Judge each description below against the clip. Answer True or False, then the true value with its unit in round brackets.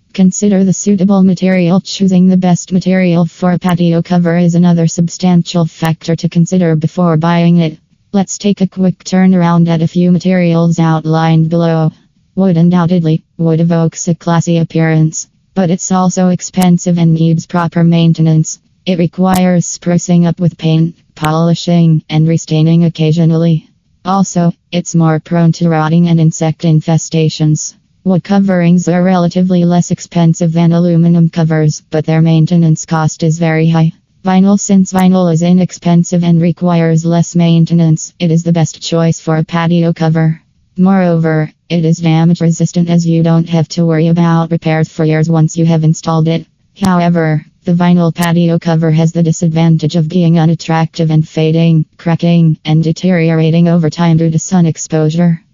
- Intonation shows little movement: True (1.4 semitones)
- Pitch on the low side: False (170 Hz)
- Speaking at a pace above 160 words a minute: False (155 wpm)